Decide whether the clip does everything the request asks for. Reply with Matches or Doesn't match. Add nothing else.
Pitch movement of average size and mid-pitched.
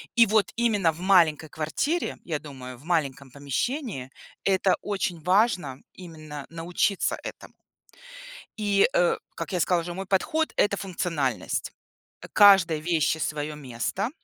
Matches